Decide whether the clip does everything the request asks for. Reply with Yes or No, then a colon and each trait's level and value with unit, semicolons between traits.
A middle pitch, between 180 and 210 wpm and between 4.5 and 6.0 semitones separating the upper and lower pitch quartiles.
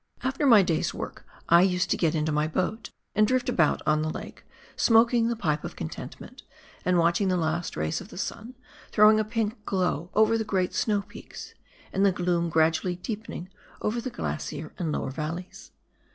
Yes: medium, 180 Hz; average, 185 wpm; average, 4.9 semitones